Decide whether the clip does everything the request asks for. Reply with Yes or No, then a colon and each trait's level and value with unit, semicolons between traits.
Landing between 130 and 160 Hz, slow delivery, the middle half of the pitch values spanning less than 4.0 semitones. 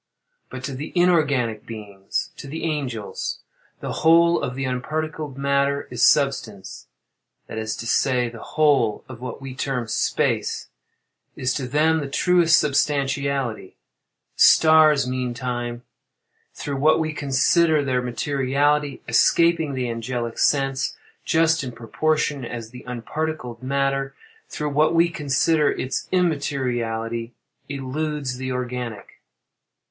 Yes: low, 135 Hz; slow, 115 wpm; average, 3.4 semitones